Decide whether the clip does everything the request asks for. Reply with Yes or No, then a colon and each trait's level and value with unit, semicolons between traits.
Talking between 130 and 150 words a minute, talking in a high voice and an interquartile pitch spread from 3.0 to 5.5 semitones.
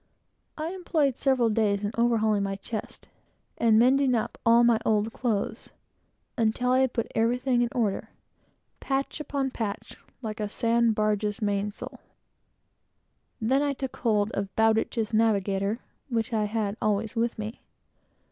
No: average, 140 wpm; high, 225 Hz; narrow, 2.6 semitones